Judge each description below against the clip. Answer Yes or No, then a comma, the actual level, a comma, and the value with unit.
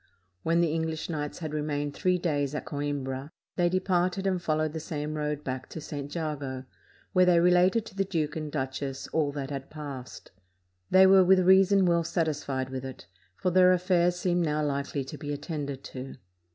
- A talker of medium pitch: Yes, medium, 155 Hz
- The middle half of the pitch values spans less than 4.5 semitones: Yes, average, 3.8 semitones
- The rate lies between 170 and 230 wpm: Yes, average, 185 wpm